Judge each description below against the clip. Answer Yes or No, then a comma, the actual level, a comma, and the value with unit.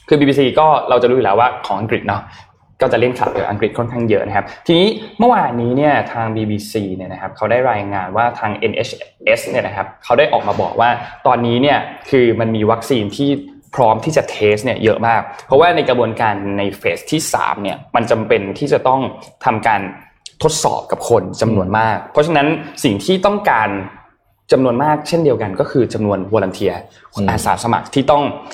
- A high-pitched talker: No, low, 120 Hz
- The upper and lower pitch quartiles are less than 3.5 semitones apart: No, average, 5.3 semitones